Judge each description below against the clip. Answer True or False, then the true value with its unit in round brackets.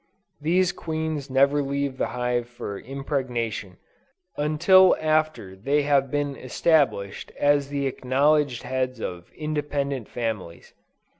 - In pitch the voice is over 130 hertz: True (140 Hz)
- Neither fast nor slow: False (115 wpm)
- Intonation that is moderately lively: True (3.3 semitones)